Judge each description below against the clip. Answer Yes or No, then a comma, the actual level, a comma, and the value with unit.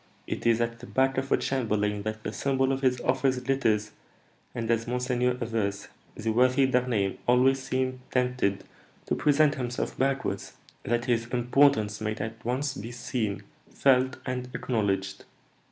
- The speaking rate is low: No, average, 155 wpm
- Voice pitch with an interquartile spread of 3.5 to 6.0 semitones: No, average, 2.9 semitones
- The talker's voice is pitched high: No, low, 125 Hz